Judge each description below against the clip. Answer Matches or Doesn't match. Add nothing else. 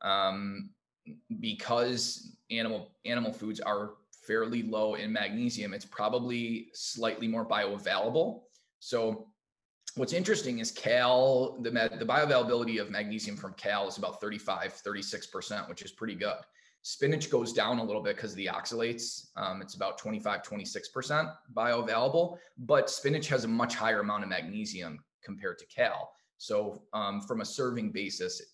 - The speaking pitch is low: Matches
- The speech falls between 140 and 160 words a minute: Matches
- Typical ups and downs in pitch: Doesn't match